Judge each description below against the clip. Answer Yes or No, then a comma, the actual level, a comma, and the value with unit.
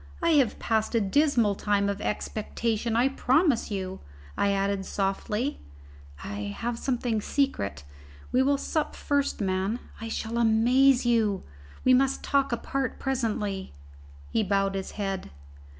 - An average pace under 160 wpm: Yes, slow, 135 wpm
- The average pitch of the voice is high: Yes, high, 225 Hz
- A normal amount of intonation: Yes, average, 4.7 semitones